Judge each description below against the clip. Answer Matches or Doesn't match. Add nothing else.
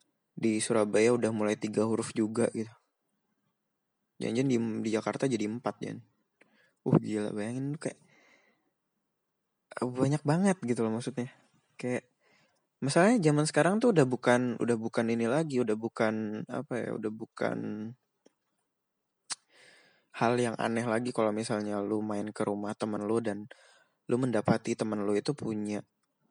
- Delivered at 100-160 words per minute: Matches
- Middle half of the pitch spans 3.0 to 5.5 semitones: Doesn't match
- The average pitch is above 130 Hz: Doesn't match